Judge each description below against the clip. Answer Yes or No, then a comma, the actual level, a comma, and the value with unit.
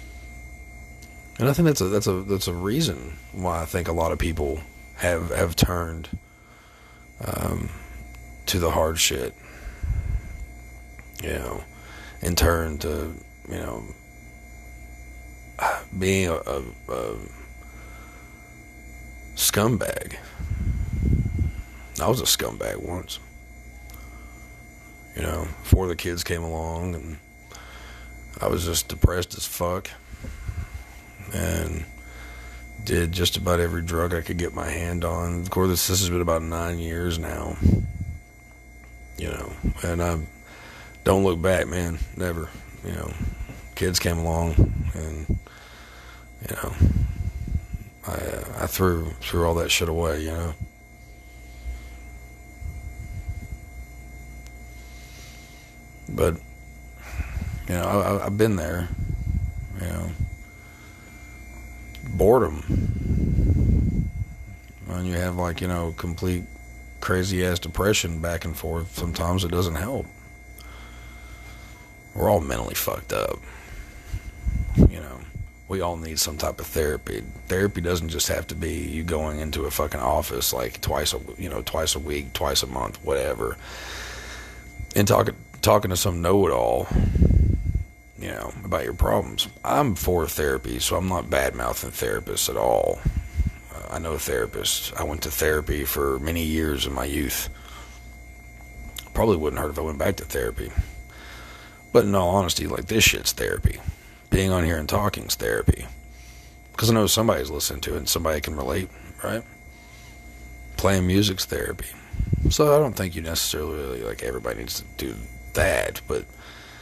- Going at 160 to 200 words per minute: No, slow, 135 wpm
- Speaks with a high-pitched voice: No, very low, 80 Hz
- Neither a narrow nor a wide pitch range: No, wide, 6.2 semitones